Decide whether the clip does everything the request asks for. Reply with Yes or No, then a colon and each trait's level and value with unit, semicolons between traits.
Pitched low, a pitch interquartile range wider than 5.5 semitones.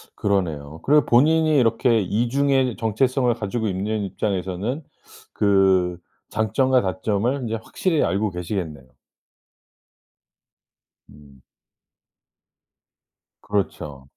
No: low, 105 Hz; average, 5.2 semitones